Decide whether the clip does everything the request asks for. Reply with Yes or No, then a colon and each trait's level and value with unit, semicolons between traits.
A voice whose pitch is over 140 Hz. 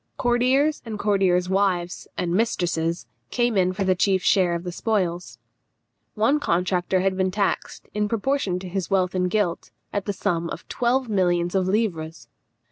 Yes: high, 190 Hz